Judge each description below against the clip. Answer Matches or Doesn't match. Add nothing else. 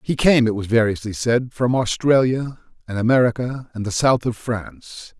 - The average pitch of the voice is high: Doesn't match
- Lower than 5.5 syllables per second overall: Matches